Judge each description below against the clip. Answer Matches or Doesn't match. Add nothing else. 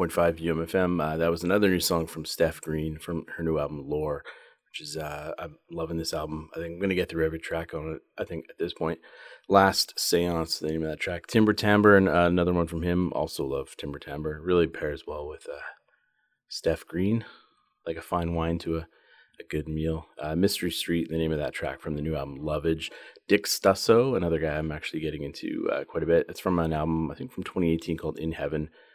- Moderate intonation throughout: Doesn't match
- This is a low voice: Matches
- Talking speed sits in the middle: Doesn't match